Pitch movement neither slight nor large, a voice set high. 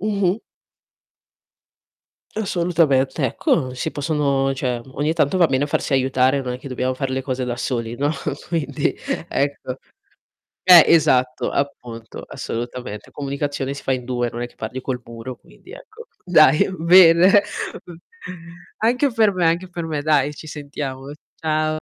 No: average, 4.2 semitones; medium, 140 Hz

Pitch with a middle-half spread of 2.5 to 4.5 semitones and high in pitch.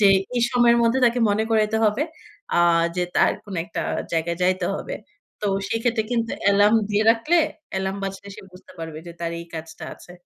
Yes: average, 4.0 semitones; high, 205 Hz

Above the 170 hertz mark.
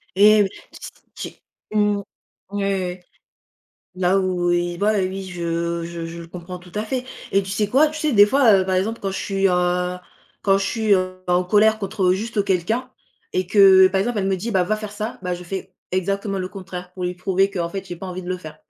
Yes: high, 190 Hz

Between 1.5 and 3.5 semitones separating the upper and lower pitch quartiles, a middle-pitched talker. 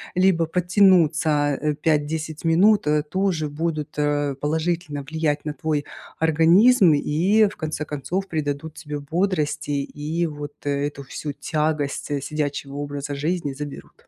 Yes: narrow, 2.4 semitones; medium, 155 Hz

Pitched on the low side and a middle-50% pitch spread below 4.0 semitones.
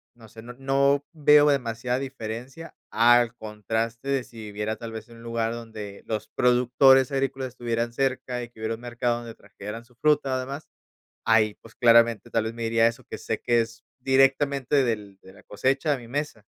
Yes: low, 120 Hz; average, 2.8 semitones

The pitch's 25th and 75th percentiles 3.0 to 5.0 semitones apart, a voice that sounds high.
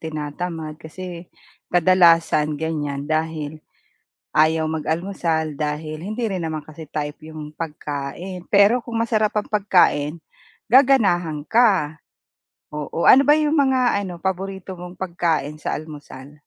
No: average, 4.0 semitones; medium, 165 Hz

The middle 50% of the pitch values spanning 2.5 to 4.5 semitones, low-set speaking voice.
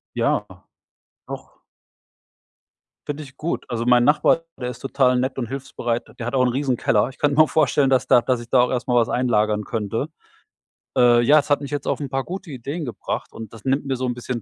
Yes: average, 2.8 semitones; low, 130 Hz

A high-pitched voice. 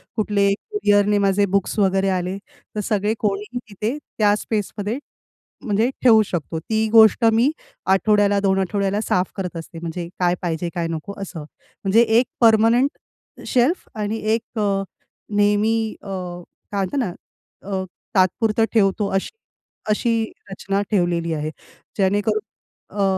Yes: high, 205 Hz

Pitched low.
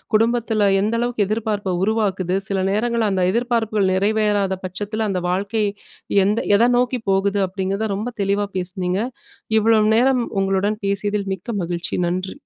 No: high, 205 Hz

